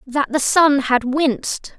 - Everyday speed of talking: Yes, average, 170 wpm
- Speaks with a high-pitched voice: Yes, very high, 275 Hz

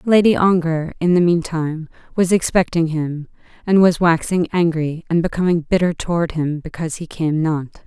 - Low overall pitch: No, medium, 165 Hz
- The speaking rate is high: No, average, 160 wpm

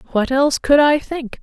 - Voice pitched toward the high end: Yes, very high, 275 Hz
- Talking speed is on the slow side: No, fast, 210 wpm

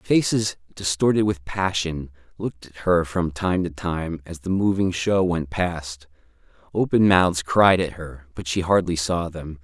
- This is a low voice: Yes, very low, 85 Hz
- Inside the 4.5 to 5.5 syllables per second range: No, 4.2 syllables/s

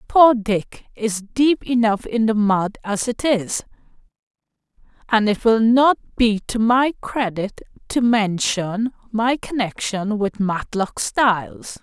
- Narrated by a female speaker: Yes, female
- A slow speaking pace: Yes, slow, 130 wpm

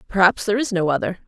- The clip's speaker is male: No, female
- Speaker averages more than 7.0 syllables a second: Yes, 7.5 syllables/s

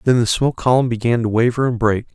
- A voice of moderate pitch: No, low, 120 Hz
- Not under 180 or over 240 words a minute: No, fast, 250 wpm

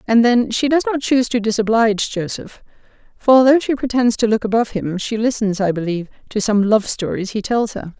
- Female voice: Yes, female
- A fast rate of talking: Yes, fast, 210 wpm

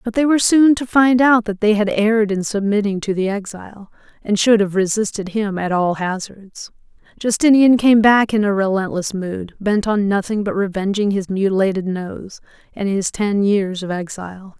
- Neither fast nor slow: Yes, average, 185 wpm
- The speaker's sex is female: Yes, female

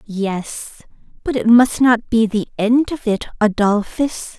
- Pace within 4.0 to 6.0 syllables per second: No, 3.7 syllables/s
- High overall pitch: Yes, high, 225 Hz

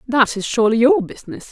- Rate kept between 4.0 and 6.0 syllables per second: No, 6.6 syllables/s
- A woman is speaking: Yes, female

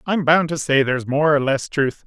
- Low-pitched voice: No, medium, 145 Hz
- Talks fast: Yes, fast, 260 wpm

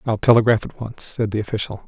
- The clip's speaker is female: No, male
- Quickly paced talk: Yes, fast, 225 wpm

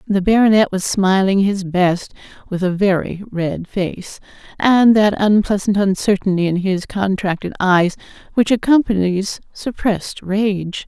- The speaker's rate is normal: No, slow, 125 wpm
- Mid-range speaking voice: No, high, 195 Hz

